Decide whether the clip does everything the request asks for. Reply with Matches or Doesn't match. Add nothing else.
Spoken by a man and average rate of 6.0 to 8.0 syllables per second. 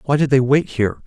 Matches